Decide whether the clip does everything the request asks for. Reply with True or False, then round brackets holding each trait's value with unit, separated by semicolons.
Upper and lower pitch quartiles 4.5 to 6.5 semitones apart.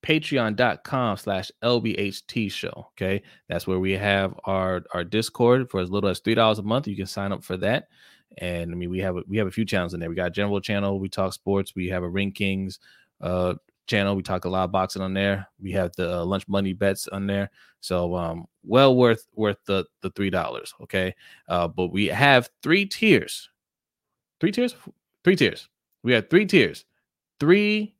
False (3.2 semitones)